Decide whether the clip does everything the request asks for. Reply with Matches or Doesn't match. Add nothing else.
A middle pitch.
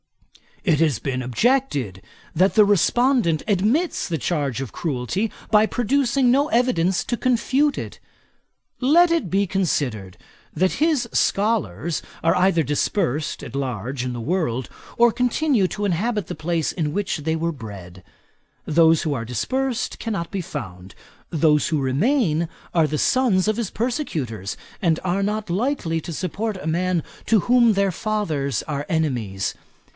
Matches